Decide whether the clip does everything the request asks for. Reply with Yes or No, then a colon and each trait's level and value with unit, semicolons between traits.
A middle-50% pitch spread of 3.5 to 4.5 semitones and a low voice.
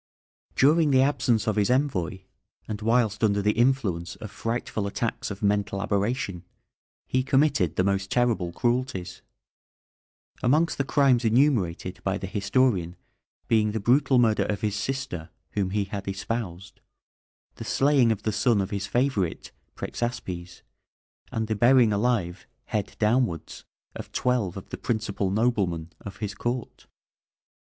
Yes: average, 4.1 semitones; low, 110 Hz